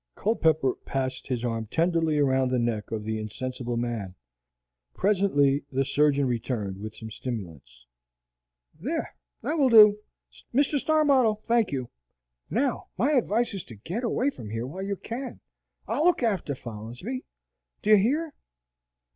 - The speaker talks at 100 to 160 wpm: Yes, average, 145 wpm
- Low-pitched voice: No, medium, 145 Hz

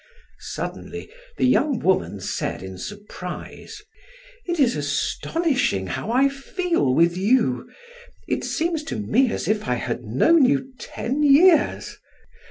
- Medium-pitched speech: No, high, 245 Hz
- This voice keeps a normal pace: No, slow, 130 wpm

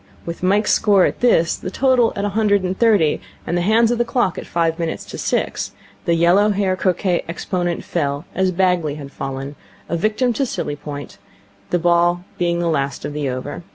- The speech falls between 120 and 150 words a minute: No, average, 200 wpm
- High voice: No, medium, 175 Hz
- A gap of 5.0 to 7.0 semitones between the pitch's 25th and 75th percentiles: No, average, 3.8 semitones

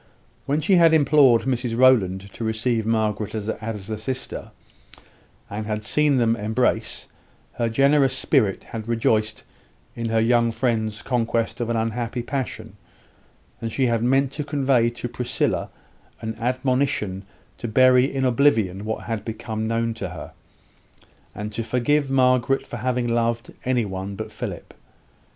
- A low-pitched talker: Yes, low, 115 Hz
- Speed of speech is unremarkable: Yes, average, 145 wpm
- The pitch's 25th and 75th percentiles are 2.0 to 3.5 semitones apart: Yes, average, 2.7 semitones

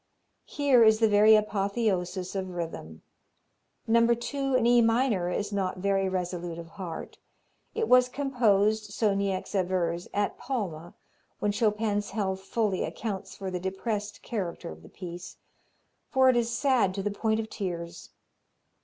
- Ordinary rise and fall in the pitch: Yes, average, 3.6 semitones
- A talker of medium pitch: No, high, 205 Hz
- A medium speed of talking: Yes, average, 150 wpm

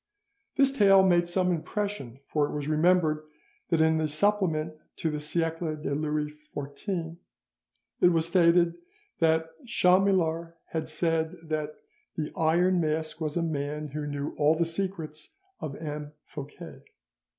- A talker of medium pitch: Yes, medium, 160 Hz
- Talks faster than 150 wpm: No, average, 140 wpm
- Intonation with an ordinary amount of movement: No, narrow, 2.3 semitones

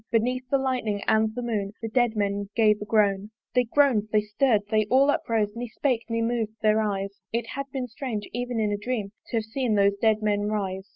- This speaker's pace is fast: Yes, fast, 220 wpm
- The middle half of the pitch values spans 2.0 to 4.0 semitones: Yes, average, 2.8 semitones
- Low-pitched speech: No, high, 220 Hz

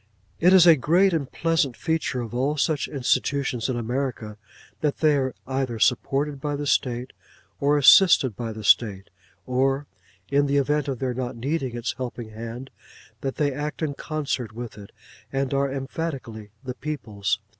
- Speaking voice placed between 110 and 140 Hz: Yes, low, 135 Hz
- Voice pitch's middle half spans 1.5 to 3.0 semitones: No, average, 3.4 semitones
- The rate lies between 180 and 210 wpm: No, average, 165 wpm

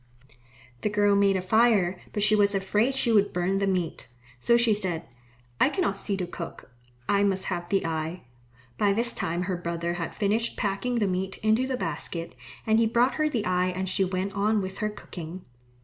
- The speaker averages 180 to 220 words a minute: Yes, average, 200 wpm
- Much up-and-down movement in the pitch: No, average, 3.1 semitones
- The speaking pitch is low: No, high, 195 Hz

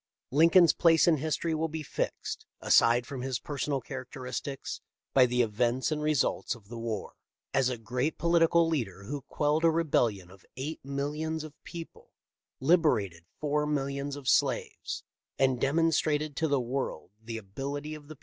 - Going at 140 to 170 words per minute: Yes, average, 165 wpm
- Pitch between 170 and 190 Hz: No, medium, 140 Hz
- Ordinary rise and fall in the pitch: Yes, average, 4.0 semitones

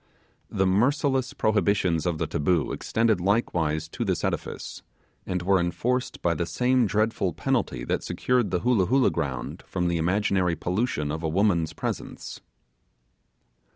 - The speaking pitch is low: Yes, very low, 95 Hz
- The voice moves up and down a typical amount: Yes, average, 5.0 semitones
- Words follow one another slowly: No, average, 145 wpm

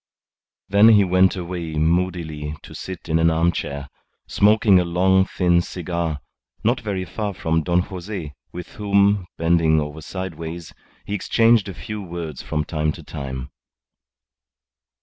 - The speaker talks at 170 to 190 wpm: No, average, 140 wpm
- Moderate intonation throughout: Yes, average, 3.2 semitones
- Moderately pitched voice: No, very low, 85 Hz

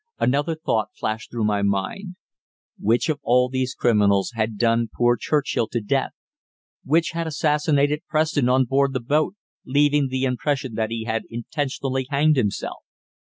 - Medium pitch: No, low, 130 Hz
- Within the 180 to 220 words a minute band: No, average, 155 wpm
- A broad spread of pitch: No, average, 4.3 semitones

